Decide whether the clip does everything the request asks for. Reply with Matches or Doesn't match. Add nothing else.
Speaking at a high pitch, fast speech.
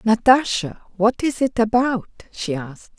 Doesn't match